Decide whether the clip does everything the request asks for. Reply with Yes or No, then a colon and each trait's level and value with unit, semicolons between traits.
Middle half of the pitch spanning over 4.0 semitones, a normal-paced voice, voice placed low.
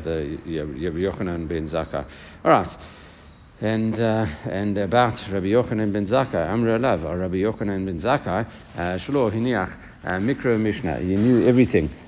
Yes: average, 5.2 semitones; average, 180 wpm; very low, 95 Hz